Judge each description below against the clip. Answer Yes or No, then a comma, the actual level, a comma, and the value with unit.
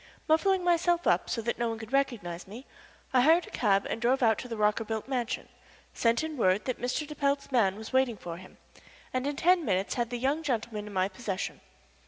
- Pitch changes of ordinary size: Yes, average, 4.8 semitones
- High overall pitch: Yes, high, 240 Hz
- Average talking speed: No, fast, 220 wpm